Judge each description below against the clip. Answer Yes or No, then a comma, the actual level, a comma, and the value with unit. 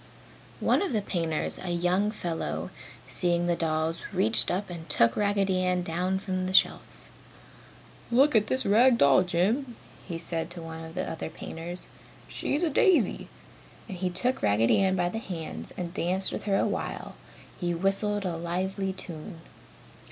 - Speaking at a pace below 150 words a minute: No, average, 165 wpm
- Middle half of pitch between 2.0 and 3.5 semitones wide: Yes, average, 3.1 semitones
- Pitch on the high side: No, medium, 180 Hz